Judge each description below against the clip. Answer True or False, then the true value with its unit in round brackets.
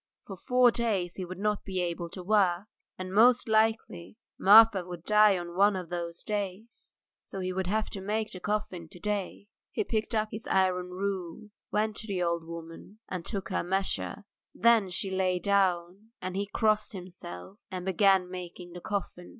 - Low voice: False (190 Hz)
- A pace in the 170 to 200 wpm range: True (185 wpm)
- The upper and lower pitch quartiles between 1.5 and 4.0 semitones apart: True (2.9 semitones)